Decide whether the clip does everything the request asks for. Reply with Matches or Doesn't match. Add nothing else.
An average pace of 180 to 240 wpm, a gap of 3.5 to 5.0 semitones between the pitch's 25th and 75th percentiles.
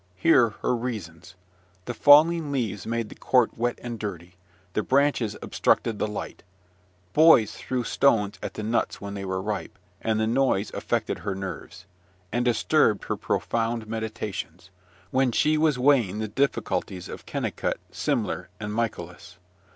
Doesn't match